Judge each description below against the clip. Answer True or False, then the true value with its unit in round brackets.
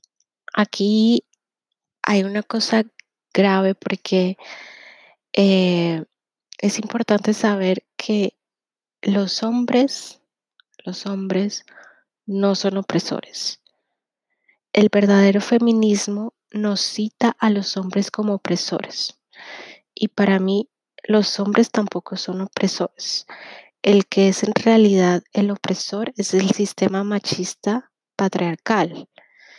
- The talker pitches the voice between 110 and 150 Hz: False (200 Hz)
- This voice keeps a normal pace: False (95 wpm)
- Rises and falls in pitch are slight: True (1.9 semitones)